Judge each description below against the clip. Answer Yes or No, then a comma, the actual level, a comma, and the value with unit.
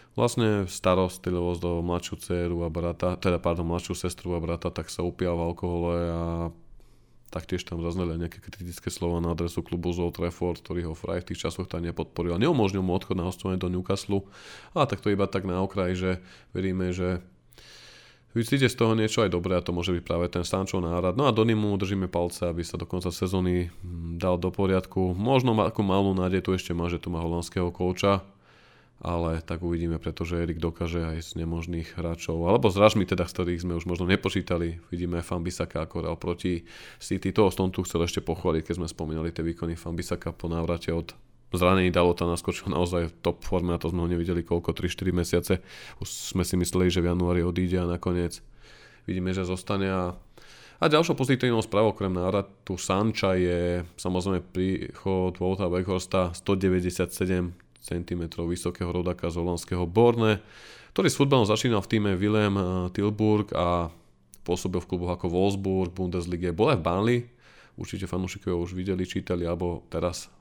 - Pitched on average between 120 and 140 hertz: No, very low, 90 Hz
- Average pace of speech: No, fast, 180 wpm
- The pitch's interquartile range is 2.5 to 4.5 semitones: No, narrow, 1.8 semitones